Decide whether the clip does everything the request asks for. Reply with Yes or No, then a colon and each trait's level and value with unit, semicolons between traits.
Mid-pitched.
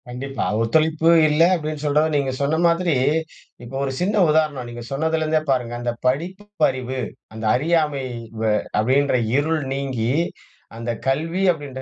Yes: medium, 145 Hz